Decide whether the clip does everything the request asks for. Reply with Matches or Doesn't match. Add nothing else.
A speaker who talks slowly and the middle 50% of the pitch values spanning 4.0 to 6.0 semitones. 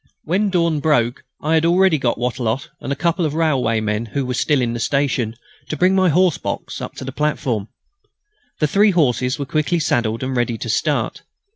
Doesn't match